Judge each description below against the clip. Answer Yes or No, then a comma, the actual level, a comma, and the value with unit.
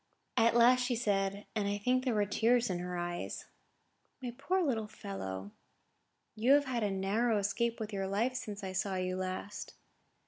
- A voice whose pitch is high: Yes, high, 210 Hz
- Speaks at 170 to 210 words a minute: Yes, average, 180 wpm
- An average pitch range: Yes, average, 3.7 semitones